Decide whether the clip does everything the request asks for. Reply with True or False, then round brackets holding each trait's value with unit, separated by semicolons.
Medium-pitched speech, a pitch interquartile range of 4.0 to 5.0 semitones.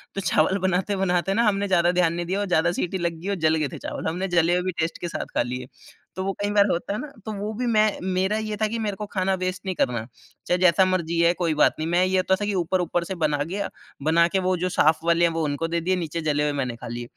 False (180 Hz; 2.7 semitones)